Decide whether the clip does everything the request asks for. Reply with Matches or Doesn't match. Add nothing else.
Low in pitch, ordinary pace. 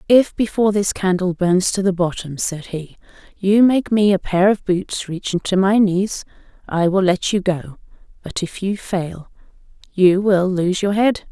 Doesn't match